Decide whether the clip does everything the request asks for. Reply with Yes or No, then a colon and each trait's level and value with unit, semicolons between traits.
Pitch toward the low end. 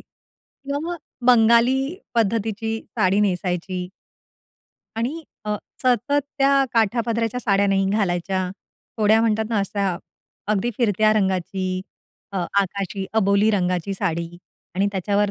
No: high, 205 Hz